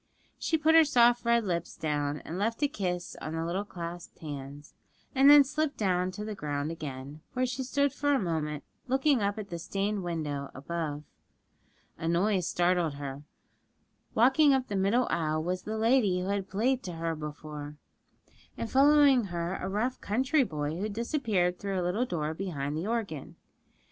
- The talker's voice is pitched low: No, high, 190 Hz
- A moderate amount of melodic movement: No, wide, 7.0 semitones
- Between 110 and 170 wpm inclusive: No, average, 180 wpm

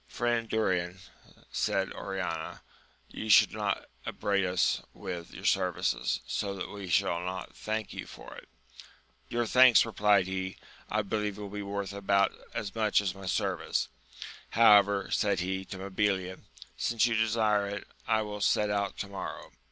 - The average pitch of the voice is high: No, low, 100 Hz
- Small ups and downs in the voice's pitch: Yes, narrow, 2.1 semitones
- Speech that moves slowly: No, average, 155 wpm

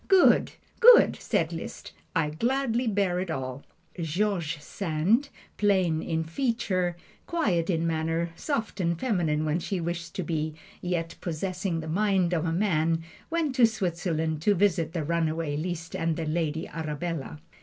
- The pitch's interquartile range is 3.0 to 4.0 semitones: Yes, average, 3.7 semitones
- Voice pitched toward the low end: No, medium, 170 Hz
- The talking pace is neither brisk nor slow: Yes, average, 150 wpm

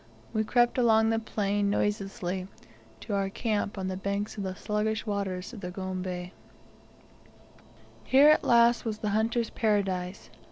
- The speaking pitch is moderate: No, high, 205 Hz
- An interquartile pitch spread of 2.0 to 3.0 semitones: Yes, average, 2.7 semitones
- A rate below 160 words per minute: Yes, average, 150 wpm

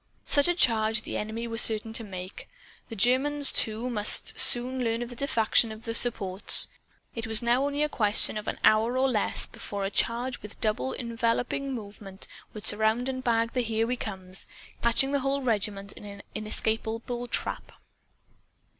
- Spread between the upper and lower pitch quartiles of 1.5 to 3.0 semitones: Yes, average, 2.7 semitones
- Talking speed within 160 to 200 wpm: Yes, average, 180 wpm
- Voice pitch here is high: Yes, high, 230 Hz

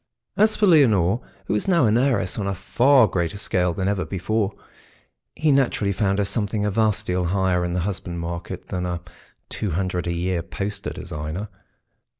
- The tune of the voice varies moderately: Yes, average, 3.5 semitones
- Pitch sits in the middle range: No, low, 100 Hz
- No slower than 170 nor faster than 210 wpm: Yes, average, 180 wpm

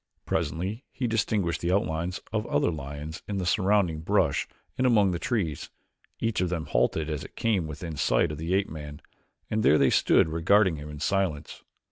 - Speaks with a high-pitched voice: No, very low, 85 Hz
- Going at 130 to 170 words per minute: No, average, 185 wpm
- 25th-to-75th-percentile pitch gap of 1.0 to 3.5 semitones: No, average, 4.7 semitones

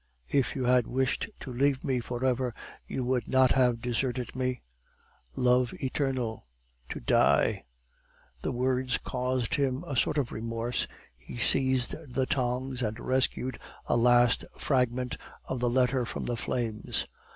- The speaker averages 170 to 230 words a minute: No, average, 150 wpm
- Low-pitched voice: Yes, low, 125 Hz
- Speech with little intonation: Yes, narrow, 1.4 semitones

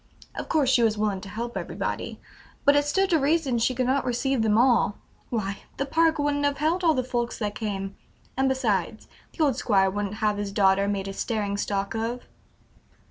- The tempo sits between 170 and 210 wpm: Yes, average, 200 wpm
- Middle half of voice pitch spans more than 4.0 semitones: Yes, average, 5.2 semitones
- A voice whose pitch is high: Yes, high, 235 Hz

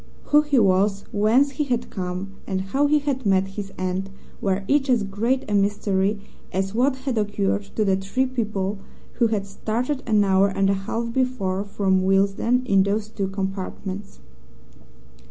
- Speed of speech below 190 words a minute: Yes, average, 170 wpm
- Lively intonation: No, average, 3.8 semitones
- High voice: Yes, high, 205 Hz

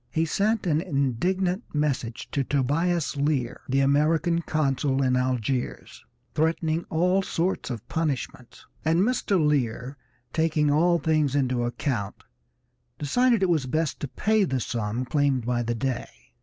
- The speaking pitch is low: No, medium, 145 Hz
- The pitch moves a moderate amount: Yes, average, 4.4 semitones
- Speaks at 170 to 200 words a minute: No, average, 140 wpm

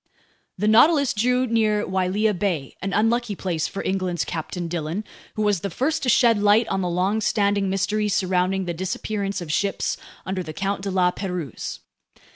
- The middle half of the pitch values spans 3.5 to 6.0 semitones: No, average, 2.9 semitones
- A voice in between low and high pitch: No, high, 195 Hz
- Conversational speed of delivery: Yes, average, 170 wpm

